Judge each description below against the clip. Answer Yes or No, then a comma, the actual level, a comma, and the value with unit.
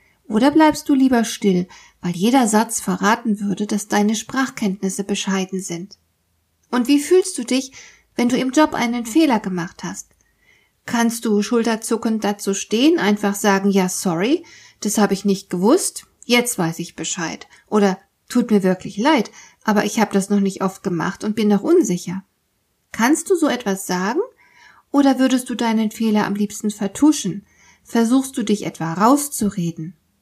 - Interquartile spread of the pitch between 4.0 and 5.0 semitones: Yes, average, 4.5 semitones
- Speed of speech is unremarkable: Yes, average, 160 wpm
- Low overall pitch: No, high, 210 Hz